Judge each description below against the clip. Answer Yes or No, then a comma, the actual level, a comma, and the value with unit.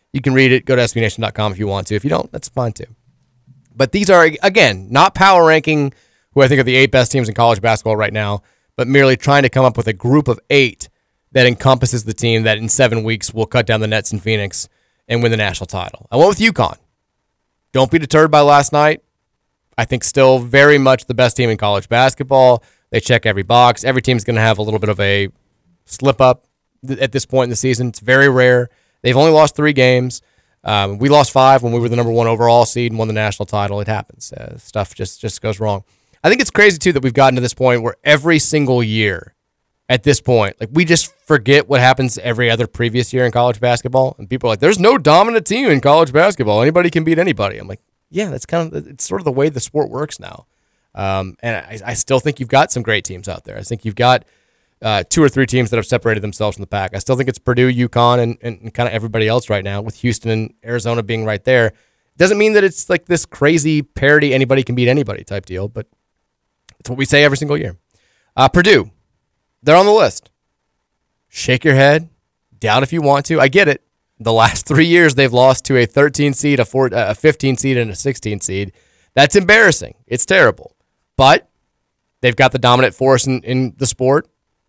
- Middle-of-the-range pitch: No, low, 125 Hz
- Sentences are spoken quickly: Yes, fast, 230 wpm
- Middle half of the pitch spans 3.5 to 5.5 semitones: Yes, average, 3.8 semitones